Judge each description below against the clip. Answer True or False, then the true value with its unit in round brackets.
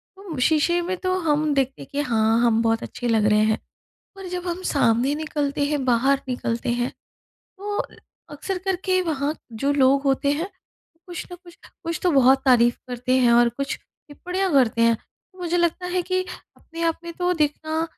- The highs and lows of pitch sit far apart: True (5.9 semitones)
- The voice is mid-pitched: False (290 Hz)